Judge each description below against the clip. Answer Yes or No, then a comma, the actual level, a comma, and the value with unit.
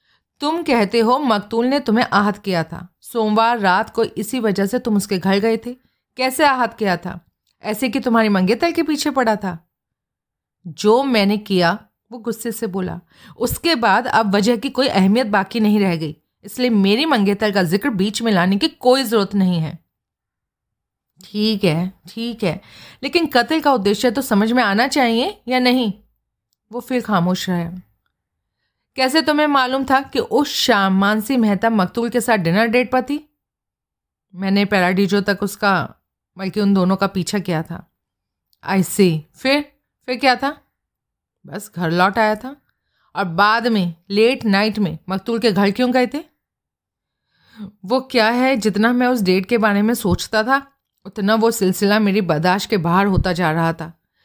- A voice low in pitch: No, high, 215 Hz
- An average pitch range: Yes, average, 4.5 semitones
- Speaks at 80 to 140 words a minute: No, average, 170 wpm